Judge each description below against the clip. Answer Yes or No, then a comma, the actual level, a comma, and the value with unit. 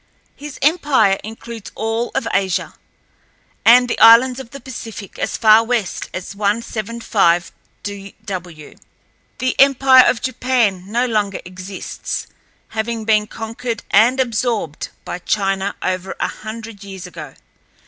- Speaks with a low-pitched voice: No, high, 220 Hz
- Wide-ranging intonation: No, average, 3.4 semitones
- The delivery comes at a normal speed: No, slow, 120 wpm